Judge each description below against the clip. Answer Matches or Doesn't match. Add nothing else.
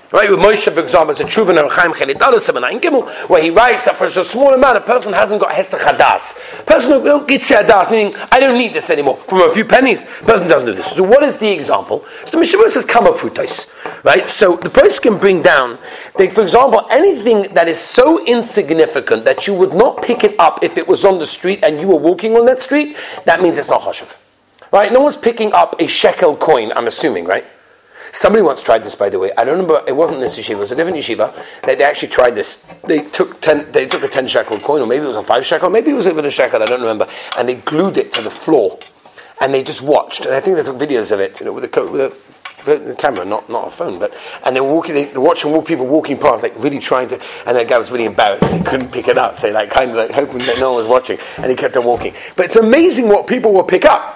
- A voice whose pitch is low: Doesn't match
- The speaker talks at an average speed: Doesn't match